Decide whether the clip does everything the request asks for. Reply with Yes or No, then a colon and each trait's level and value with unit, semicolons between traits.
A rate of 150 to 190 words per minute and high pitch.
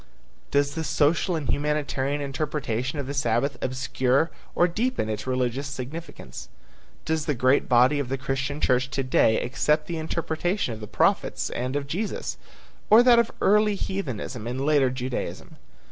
No: average, 160 wpm; medium, 140 Hz